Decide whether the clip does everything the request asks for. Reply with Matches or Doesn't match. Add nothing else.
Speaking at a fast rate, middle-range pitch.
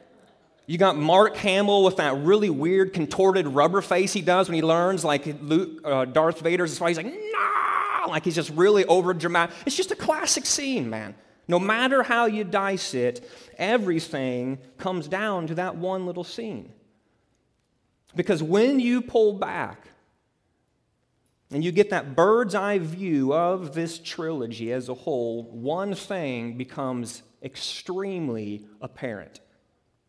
Doesn't match